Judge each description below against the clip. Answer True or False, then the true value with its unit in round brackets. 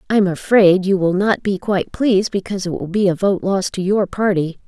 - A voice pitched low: False (190 Hz)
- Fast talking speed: True (245 wpm)